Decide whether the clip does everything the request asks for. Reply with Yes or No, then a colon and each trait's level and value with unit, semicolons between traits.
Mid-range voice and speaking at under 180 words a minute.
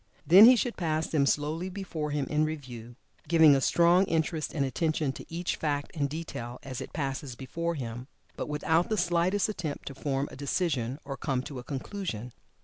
No: medium, 150 Hz; average, 190 wpm